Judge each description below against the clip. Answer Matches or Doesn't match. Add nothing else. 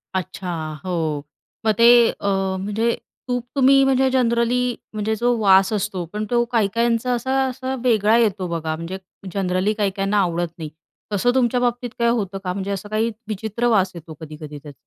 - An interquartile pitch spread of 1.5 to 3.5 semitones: Doesn't match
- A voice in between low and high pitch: Doesn't match